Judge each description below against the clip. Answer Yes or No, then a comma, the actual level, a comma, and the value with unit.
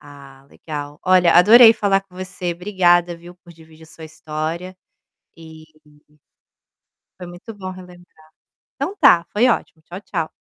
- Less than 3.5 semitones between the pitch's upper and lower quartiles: Yes, average, 2.7 semitones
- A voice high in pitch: No, medium, 175 Hz